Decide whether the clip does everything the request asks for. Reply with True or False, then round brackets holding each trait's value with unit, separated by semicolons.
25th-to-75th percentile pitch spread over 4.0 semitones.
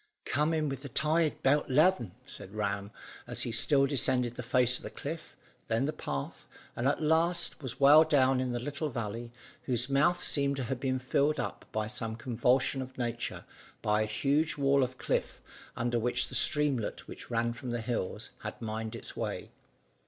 False (3.4 semitones)